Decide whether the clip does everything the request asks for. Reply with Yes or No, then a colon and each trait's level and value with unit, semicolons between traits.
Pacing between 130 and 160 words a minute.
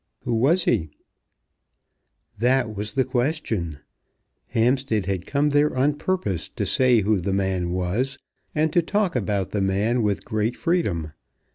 Yes: average, 145 wpm